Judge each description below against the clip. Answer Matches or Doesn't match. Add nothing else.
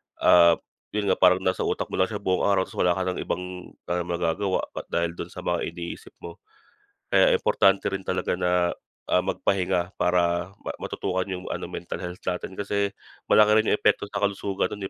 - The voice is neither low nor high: Doesn't match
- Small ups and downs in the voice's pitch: Matches